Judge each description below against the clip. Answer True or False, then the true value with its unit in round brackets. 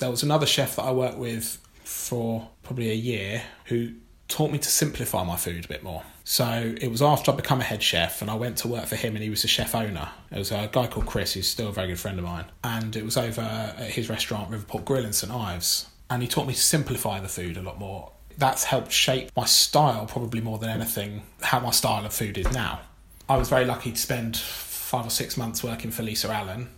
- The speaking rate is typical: False (250 wpm)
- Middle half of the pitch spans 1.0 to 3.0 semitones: False (3.5 semitones)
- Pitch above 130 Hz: False (115 Hz)